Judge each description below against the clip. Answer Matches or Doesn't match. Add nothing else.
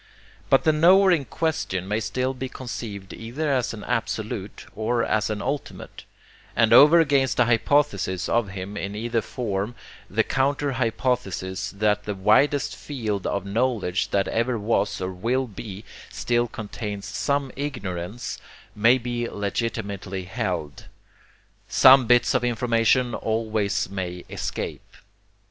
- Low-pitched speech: Matches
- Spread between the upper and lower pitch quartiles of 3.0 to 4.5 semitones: Matches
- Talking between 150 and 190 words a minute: Doesn't match